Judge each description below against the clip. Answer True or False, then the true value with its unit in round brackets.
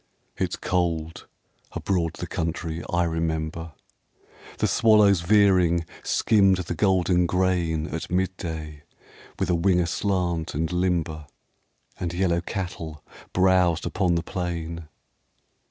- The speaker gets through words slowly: True (110 wpm)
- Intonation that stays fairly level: True (2.1 semitones)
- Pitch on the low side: True (85 Hz)